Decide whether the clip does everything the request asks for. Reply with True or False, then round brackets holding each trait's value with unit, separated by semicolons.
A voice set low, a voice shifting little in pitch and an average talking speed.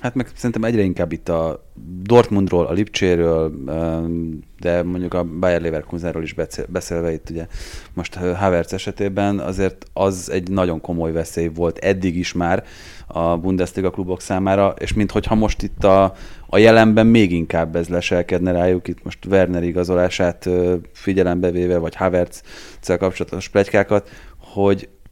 True (90 Hz; 2.3 semitones; 140 wpm)